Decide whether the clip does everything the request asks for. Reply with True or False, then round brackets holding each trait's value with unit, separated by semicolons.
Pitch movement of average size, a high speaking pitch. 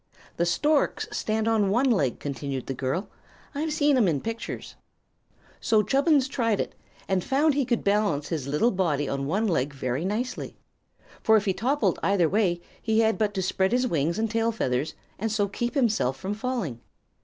False (6.6 semitones; 205 Hz)